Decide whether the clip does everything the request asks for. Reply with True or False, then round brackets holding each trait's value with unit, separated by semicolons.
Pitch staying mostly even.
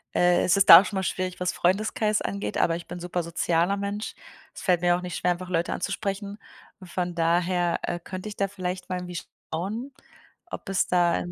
True (2.1 semitones)